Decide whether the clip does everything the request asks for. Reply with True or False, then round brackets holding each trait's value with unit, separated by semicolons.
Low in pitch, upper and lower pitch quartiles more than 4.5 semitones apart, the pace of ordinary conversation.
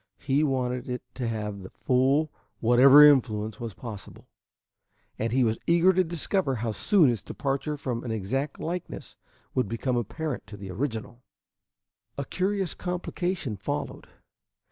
True (130 Hz; 5.0 semitones; 145 wpm)